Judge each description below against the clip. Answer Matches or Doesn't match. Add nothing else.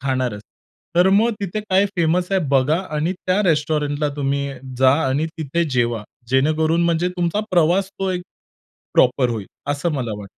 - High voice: Doesn't match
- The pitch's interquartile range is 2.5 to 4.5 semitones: Doesn't match